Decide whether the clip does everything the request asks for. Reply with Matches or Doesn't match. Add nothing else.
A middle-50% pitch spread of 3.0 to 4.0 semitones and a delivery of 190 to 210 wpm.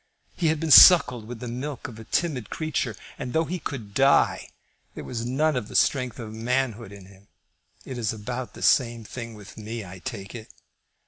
Matches